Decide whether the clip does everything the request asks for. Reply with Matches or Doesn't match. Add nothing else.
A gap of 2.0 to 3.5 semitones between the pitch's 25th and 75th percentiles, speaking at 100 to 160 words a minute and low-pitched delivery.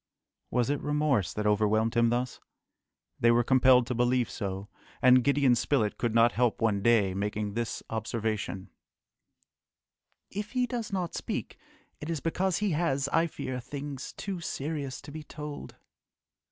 Doesn't match